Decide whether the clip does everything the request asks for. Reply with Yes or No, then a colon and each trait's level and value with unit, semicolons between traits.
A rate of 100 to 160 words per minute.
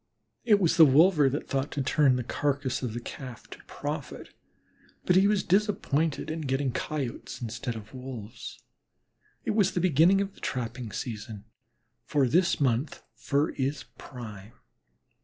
Yes: average, 155 wpm